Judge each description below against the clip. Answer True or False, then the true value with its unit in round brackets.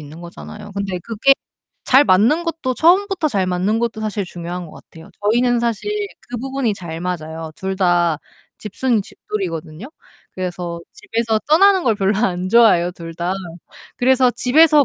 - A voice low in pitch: False (205 Hz)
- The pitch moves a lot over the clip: True (6.3 semitones)